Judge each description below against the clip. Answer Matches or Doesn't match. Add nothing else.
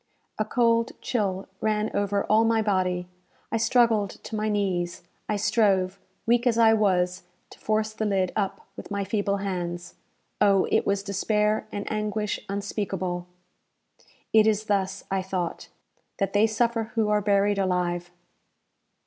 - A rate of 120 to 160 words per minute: Matches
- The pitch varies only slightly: Matches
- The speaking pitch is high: Matches